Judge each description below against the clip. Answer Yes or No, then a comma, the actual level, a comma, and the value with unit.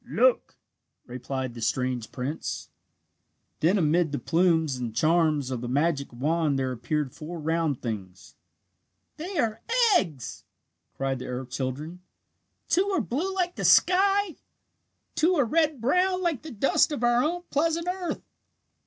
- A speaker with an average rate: Yes, average, 145 wpm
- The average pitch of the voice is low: No, medium, 165 Hz